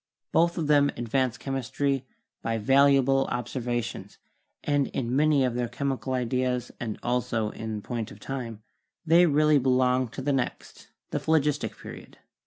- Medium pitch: No, low, 130 Hz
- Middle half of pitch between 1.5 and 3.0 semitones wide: Yes, average, 2.7 semitones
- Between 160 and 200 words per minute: No, average, 145 wpm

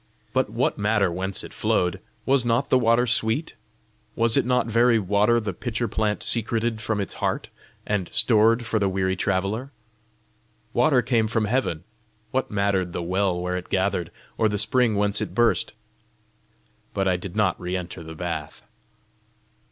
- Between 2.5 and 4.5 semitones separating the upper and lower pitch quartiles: Yes, average, 3.7 semitones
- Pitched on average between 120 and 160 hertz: No, low, 105 Hz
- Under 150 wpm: No, average, 165 wpm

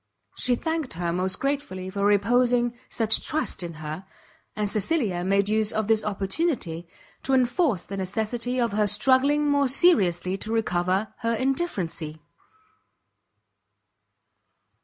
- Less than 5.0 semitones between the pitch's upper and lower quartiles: No, wide, 5.4 semitones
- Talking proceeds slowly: Yes, slow, 125 wpm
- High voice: Yes, high, 215 Hz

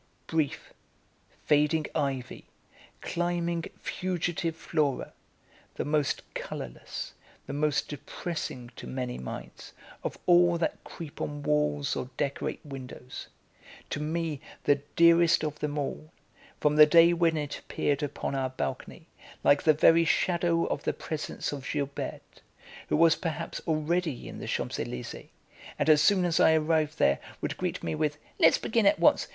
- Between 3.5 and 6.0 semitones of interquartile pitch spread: No, narrow, 2.6 semitones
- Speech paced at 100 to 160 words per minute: Yes, average, 145 wpm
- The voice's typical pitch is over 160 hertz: No, medium, 150 Hz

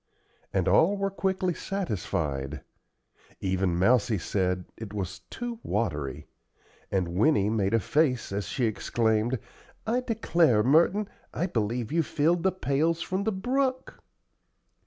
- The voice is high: No, low, 125 Hz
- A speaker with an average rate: No, slow, 130 wpm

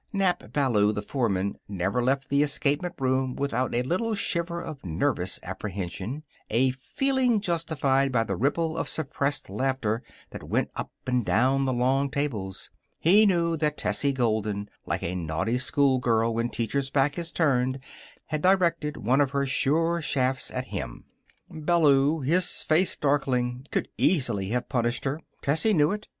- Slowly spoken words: No, average, 155 wpm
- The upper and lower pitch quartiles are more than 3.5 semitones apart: Yes, average, 4.5 semitones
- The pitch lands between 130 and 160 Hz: Yes, low, 135 Hz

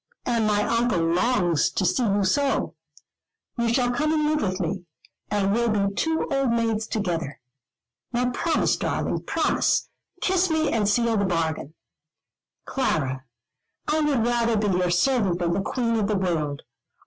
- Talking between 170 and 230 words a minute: No, average, 160 wpm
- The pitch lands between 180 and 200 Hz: No, high, 215 Hz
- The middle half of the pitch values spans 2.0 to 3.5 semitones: No, average, 5.3 semitones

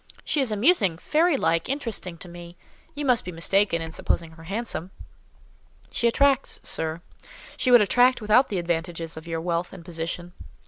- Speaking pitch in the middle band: Yes, medium, 180 Hz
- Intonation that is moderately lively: No, wide, 6.6 semitones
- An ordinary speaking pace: Yes, average, 165 wpm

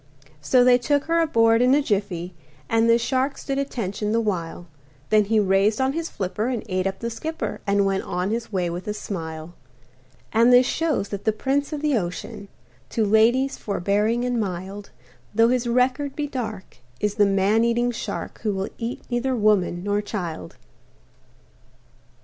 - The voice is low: No, high, 220 Hz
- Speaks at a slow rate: No, average, 175 wpm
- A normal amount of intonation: Yes, average, 4.1 semitones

